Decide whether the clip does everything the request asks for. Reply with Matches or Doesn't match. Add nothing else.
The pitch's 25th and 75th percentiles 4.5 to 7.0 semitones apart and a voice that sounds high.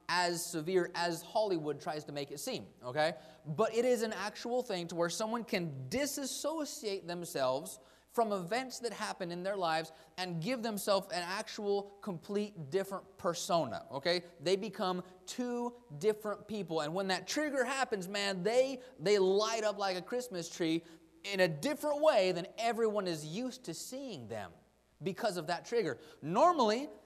Matches